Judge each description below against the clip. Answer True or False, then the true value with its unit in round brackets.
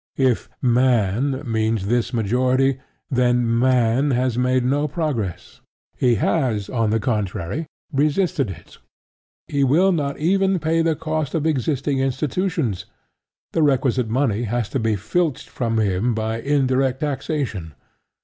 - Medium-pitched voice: False (130 Hz)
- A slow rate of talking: True (130 wpm)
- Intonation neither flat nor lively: True (4.3 semitones)